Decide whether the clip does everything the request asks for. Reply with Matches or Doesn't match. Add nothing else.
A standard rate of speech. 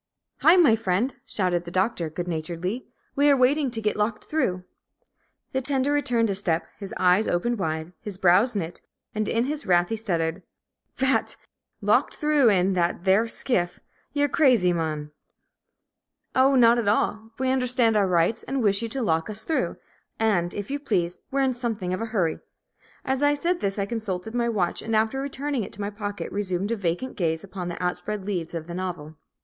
Doesn't match